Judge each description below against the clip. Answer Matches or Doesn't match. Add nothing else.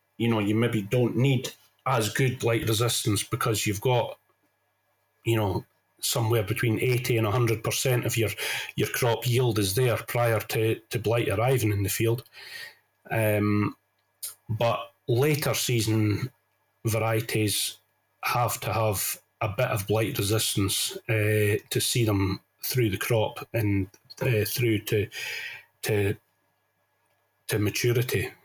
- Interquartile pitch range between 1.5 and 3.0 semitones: Matches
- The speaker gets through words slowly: Matches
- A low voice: Matches